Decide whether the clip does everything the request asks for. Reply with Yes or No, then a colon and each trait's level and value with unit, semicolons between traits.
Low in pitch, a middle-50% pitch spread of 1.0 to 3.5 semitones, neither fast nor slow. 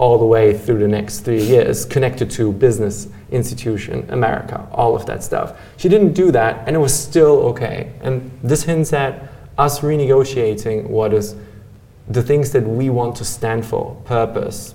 No: low, 120 Hz; average, 4.0 semitones; average, 175 wpm